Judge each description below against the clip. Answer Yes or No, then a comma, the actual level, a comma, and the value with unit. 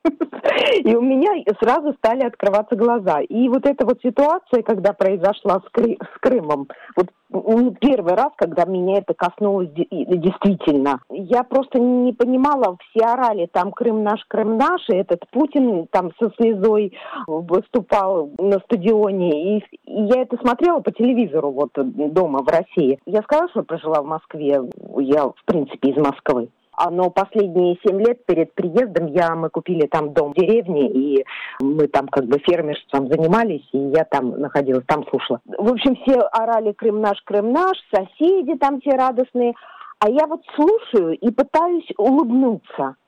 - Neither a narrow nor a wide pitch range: No, wide, 7.1 semitones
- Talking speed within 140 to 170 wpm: Yes, average, 155 wpm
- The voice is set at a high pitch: Yes, high, 210 Hz